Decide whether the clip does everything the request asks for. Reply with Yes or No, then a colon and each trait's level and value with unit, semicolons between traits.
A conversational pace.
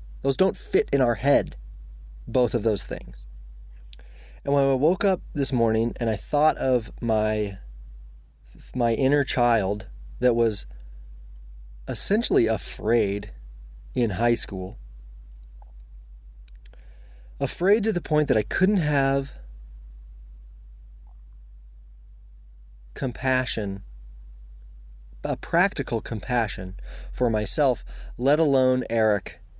No: slow, 100 wpm